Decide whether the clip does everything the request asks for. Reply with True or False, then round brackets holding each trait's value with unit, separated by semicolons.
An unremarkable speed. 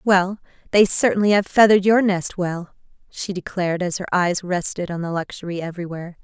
True (175 wpm)